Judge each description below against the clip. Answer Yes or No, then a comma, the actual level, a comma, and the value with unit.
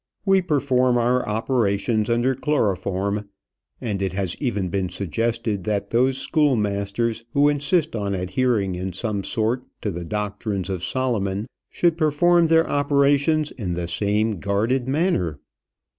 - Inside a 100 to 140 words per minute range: Yes, slow, 135 wpm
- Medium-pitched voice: No, low, 110 Hz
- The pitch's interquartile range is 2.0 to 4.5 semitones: No, wide, 5.4 semitones